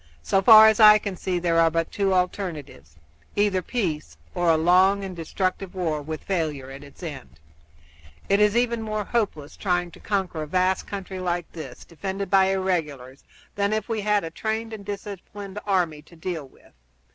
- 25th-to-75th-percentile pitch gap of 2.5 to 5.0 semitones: Yes, average, 3.9 semitones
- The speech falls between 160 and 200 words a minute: Yes, average, 180 wpm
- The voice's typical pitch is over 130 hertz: Yes, medium, 185 Hz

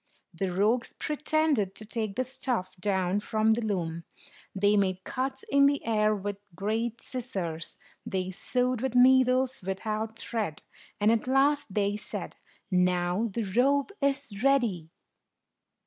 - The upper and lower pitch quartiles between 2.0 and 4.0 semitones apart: No, average, 4.9 semitones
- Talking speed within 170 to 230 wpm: No, slow, 135 wpm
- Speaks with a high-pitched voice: Yes, high, 220 Hz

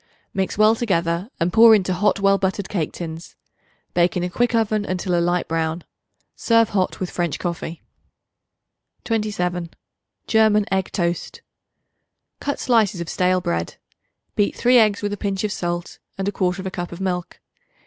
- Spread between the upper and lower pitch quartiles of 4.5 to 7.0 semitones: No, average, 3.3 semitones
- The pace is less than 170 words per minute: Yes, average, 160 wpm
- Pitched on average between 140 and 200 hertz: Yes, high, 190 Hz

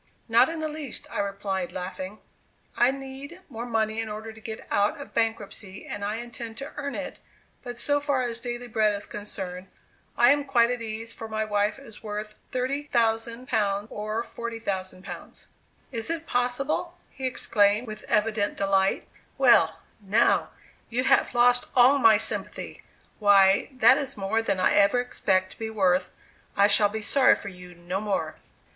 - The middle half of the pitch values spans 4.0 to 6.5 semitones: No, average, 3.4 semitones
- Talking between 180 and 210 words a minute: No, average, 165 wpm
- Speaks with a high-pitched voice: Yes, high, 225 Hz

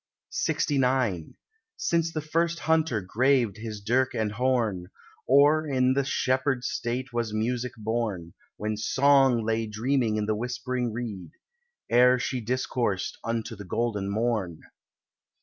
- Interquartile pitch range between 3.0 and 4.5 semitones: Yes, average, 3.4 semitones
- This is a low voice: Yes, low, 120 Hz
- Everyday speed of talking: No, slow, 130 wpm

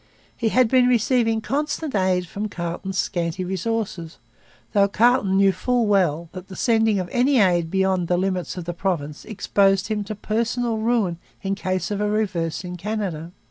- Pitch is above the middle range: Yes, high, 195 Hz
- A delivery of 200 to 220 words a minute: No, average, 175 wpm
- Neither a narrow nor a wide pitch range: Yes, average, 3.7 semitones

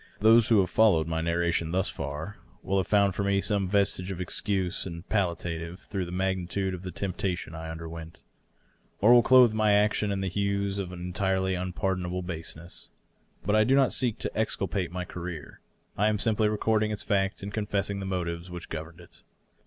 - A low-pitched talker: Yes, very low, 95 Hz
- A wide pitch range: No, average, 2.8 semitones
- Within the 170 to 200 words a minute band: Yes, average, 190 wpm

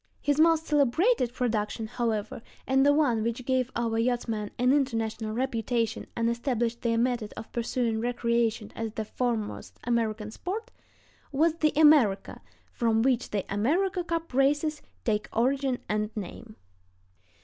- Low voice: No, high, 235 Hz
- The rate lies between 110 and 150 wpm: Yes, average, 140 wpm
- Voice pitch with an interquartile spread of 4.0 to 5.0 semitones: No, average, 3.6 semitones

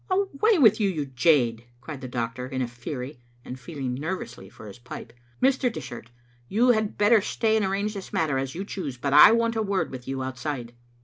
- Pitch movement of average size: No, wide, 8.9 semitones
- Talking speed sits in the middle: No, fast, 210 wpm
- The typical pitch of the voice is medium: Yes, medium, 150 Hz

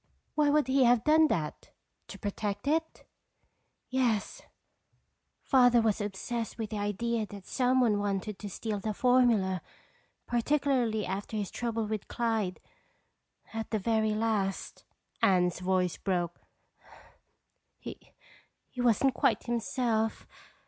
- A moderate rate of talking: No, slow, 115 wpm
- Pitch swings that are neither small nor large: Yes, average, 3.4 semitones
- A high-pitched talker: Yes, high, 220 Hz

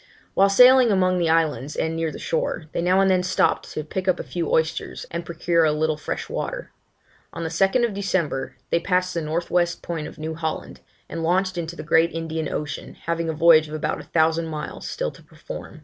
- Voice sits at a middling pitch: Yes, medium, 165 Hz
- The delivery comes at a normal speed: No, fast, 215 wpm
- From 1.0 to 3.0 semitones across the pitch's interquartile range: Yes, narrow, 2.5 semitones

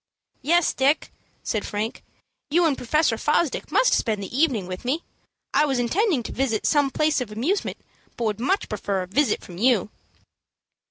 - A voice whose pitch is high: Yes, very high, 255 Hz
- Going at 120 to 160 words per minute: No, average, 170 wpm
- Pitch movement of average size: No, wide, 6.0 semitones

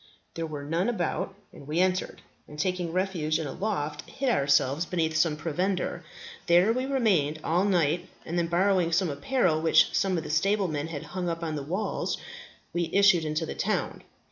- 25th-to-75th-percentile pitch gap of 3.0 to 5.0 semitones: Yes, average, 3.5 semitones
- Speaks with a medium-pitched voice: Yes, medium, 170 Hz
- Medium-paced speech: Yes, average, 185 wpm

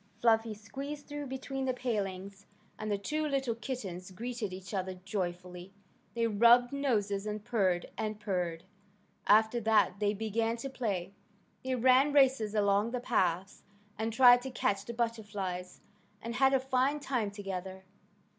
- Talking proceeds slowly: No, average, 150 wpm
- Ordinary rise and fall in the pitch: Yes, average, 4.2 semitones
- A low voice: No, high, 220 Hz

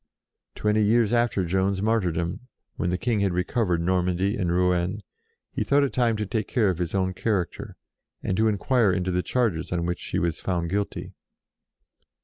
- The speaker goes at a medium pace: Yes, average, 175 wpm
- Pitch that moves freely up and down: No, average, 3.6 semitones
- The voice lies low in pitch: Yes, very low, 95 Hz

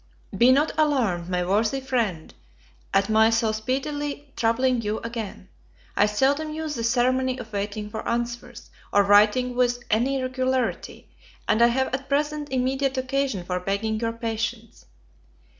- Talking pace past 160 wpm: No, average, 145 wpm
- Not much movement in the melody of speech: No, average, 3.4 semitones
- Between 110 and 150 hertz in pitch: No, high, 240 Hz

